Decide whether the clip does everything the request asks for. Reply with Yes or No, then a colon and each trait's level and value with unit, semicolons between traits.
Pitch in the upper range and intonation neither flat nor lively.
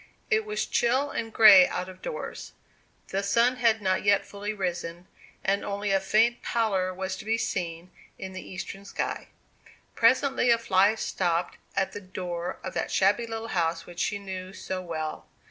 Yes: high, 195 Hz; average, 3.5 semitones